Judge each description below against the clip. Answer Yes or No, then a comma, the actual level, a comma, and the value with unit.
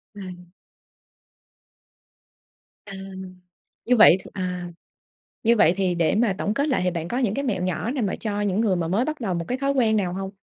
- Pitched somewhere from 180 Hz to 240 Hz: Yes, high, 200 Hz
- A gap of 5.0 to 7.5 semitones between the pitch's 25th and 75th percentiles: No, average, 4.5 semitones